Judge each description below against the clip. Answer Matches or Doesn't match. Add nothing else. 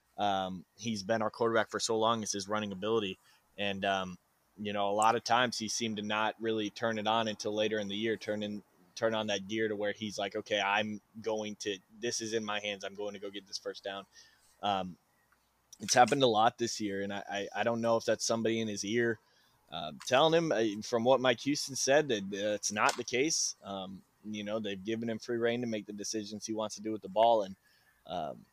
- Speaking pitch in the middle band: Doesn't match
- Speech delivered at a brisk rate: Matches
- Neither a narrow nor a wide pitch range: Doesn't match